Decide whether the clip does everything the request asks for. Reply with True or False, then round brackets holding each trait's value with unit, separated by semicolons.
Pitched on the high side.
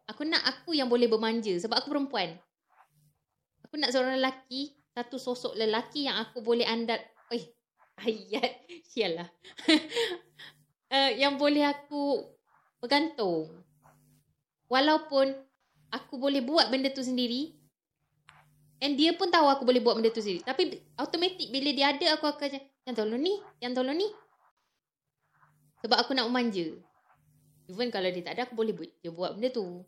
True (250 Hz)